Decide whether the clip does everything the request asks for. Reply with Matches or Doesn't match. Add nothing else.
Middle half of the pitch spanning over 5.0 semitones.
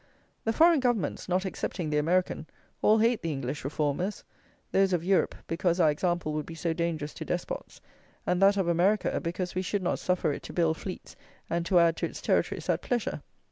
Doesn't match